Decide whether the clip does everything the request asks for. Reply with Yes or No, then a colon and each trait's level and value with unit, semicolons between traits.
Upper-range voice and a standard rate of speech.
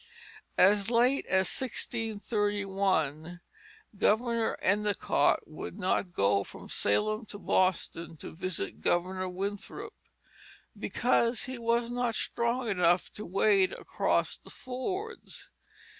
No: high, 205 Hz; slow, 105 wpm